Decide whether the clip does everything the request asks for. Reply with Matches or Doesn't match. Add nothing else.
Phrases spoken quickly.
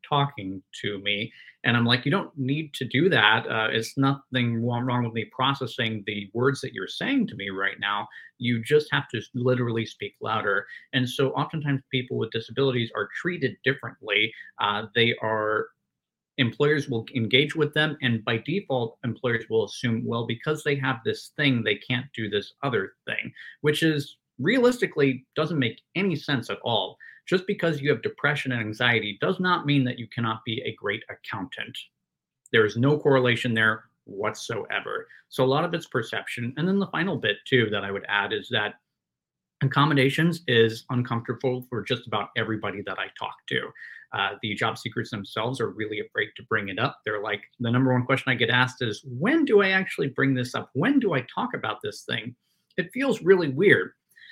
Doesn't match